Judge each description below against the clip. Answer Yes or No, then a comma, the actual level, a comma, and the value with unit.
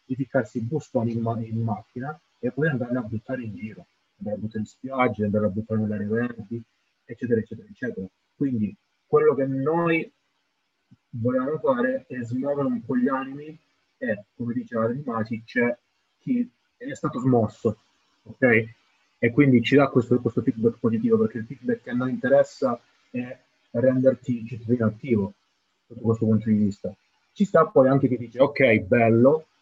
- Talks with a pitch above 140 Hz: No, low, 125 Hz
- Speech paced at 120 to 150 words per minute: No, average, 160 wpm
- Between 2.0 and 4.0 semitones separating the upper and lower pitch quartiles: Yes, average, 3.4 semitones